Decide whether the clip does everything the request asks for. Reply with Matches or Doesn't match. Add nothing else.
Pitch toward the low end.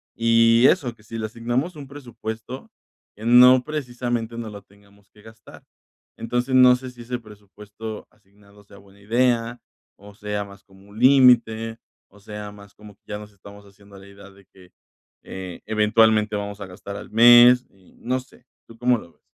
Matches